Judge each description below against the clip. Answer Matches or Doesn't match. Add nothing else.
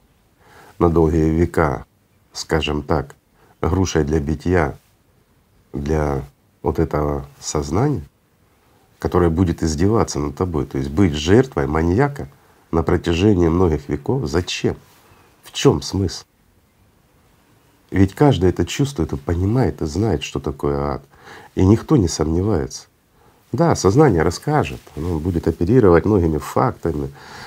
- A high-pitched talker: Doesn't match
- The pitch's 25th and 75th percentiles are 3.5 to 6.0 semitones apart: Matches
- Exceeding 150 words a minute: Doesn't match